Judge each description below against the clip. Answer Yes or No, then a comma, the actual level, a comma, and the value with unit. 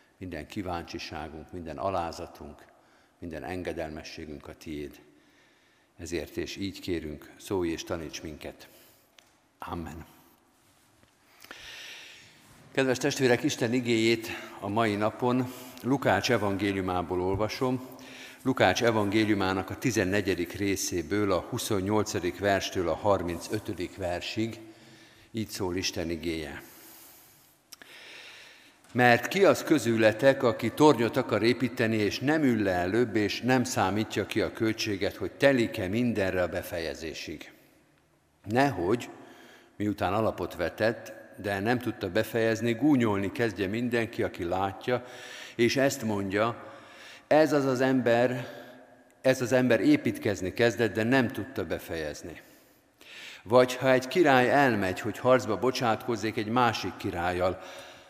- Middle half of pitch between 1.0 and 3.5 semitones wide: No, average, 4.3 semitones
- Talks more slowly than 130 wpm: Yes, average, 110 wpm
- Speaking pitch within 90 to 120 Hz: Yes, low, 110 Hz